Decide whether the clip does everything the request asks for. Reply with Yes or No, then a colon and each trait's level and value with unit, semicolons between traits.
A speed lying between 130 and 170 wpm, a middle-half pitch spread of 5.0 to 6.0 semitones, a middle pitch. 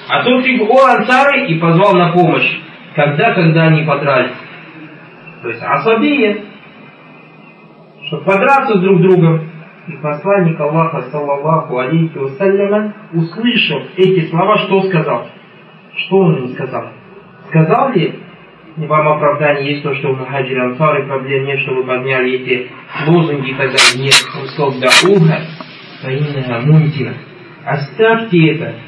Yes: average, 135 wpm; wide, 5.5 semitones; medium, 165 Hz